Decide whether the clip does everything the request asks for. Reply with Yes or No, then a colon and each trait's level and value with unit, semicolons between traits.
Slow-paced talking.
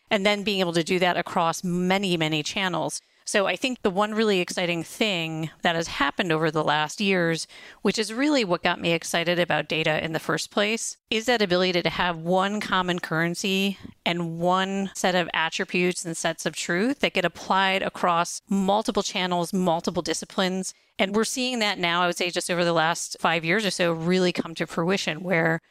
No: average, 200 wpm